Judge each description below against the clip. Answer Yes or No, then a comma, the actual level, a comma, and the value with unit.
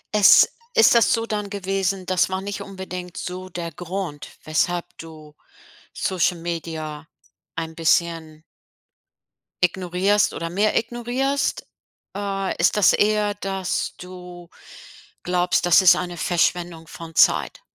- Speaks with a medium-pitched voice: Yes, medium, 180 Hz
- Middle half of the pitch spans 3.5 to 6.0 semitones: No, average, 2.8 semitones